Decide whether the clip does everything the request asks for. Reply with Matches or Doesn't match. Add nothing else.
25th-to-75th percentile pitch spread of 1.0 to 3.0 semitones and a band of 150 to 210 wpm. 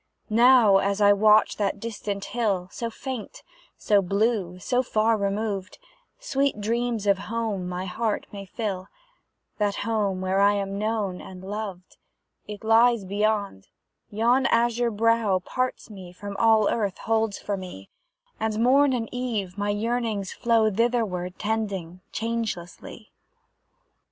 Doesn't match